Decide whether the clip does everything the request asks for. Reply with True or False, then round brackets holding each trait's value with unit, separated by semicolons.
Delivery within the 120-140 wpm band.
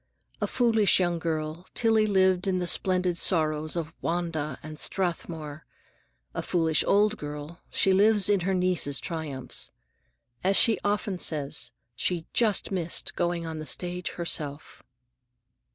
True (135 wpm)